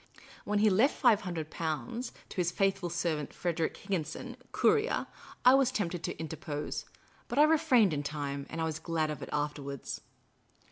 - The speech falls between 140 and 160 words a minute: No, average, 170 wpm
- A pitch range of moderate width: No, wide, 6.7 semitones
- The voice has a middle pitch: Yes, medium, 175 Hz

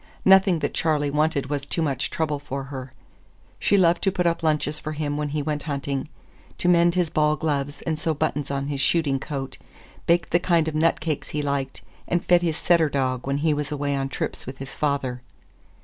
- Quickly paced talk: Yes, fast, 210 wpm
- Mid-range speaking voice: Yes, medium, 150 Hz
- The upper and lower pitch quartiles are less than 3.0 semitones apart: Yes, narrow, 2.6 semitones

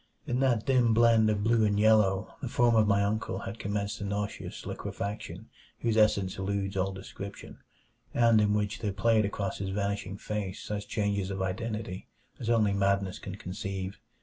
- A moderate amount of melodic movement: No, narrow, 2.0 semitones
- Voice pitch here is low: Yes, low, 105 Hz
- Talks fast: No, average, 175 wpm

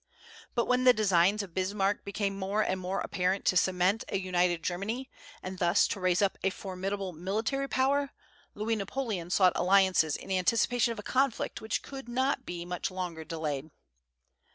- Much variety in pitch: No, average, 3.3 semitones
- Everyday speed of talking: Yes, average, 175 wpm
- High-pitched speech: Yes, high, 195 Hz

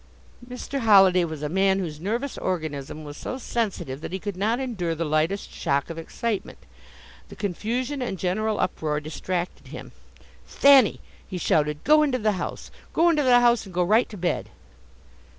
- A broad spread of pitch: Yes, wide, 6.3 semitones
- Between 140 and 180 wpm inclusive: Yes, average, 170 wpm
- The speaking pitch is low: No, high, 195 Hz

